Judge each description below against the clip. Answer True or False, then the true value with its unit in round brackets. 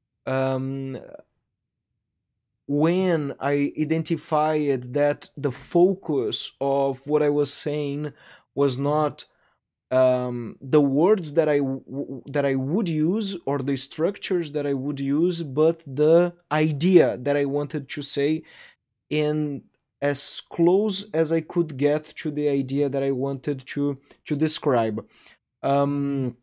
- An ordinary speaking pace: False (130 wpm)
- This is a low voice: False (145 Hz)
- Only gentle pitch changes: True (2.2 semitones)